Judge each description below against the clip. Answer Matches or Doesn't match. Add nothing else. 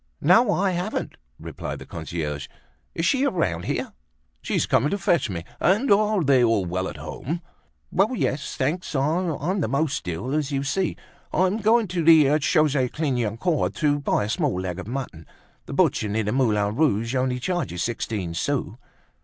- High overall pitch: Doesn't match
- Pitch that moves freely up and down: Matches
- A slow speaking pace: Doesn't match